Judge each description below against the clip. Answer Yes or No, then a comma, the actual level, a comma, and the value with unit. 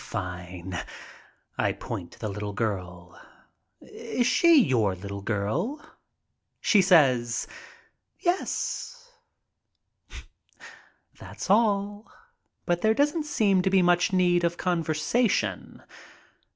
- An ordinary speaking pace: No, slow, 100 wpm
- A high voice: No, medium, 175 Hz